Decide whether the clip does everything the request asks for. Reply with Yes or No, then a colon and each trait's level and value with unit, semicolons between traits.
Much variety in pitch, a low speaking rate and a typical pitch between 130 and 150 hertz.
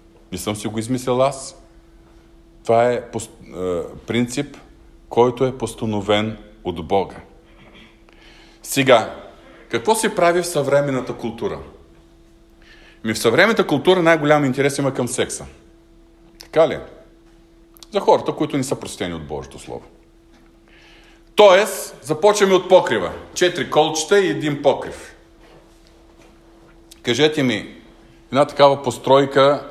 Yes: wide, 6.7 semitones; slow, 110 wpm; low, 135 Hz